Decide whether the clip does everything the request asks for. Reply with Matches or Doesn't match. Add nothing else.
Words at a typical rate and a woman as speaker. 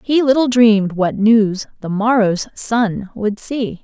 Matches